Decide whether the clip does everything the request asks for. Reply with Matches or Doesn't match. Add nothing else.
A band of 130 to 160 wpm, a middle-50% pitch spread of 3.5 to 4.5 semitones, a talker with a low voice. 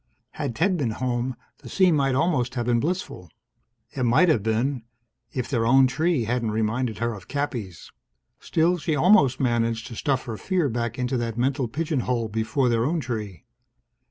Doesn't match